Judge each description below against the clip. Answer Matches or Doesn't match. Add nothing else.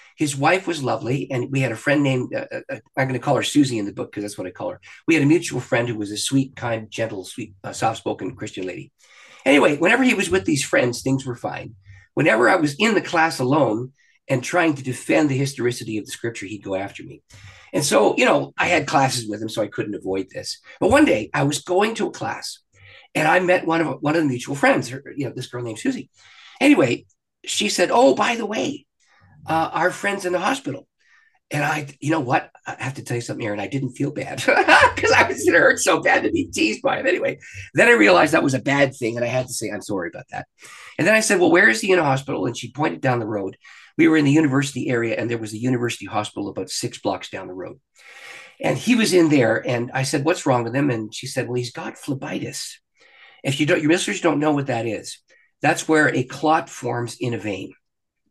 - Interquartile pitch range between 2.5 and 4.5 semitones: Doesn't match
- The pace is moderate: Doesn't match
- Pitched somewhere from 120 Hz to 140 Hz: Matches